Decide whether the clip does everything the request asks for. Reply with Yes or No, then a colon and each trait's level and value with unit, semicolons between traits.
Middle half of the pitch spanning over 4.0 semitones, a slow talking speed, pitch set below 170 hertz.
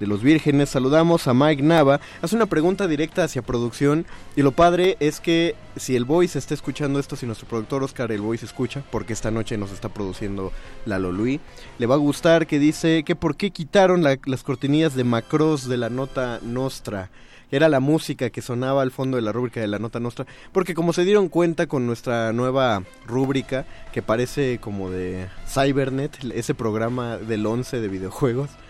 No: average, 4.6 semitones; fast, 190 wpm; low, 135 Hz